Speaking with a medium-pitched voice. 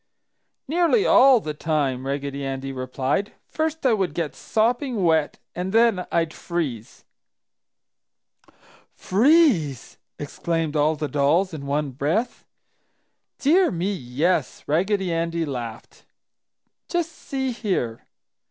Yes: medium, 165 Hz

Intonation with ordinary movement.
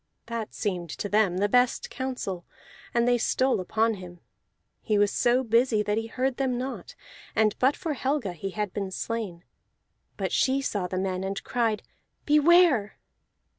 Yes: average, 4.4 semitones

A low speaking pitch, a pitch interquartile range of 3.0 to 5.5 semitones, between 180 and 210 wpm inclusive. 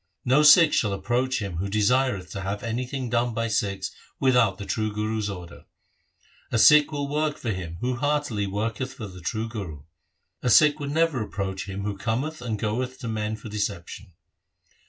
Yes: low, 110 Hz; average, 4.5 semitones; average, 185 wpm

